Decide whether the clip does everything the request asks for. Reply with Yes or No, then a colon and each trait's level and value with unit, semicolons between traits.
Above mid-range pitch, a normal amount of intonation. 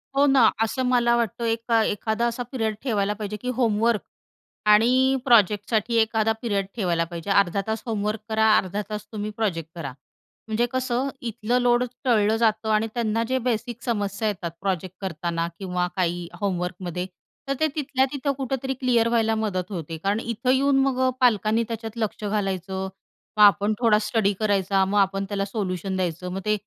Yes: high, 215 Hz; average, 3.3 semitones